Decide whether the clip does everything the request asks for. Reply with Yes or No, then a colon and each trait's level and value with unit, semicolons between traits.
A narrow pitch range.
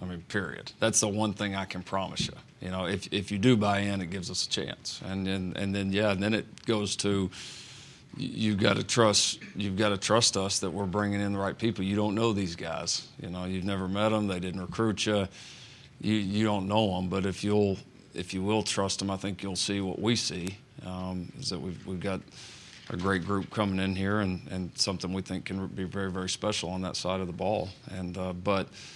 Yes: narrow, 1.9 semitones